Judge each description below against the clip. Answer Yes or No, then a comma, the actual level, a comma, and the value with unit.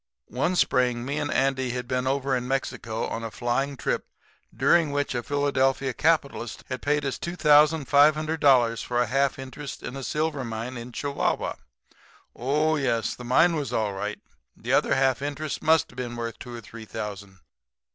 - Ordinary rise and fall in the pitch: Yes, average, 3.2 semitones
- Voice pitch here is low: Yes, low, 130 Hz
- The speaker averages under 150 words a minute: No, average, 175 wpm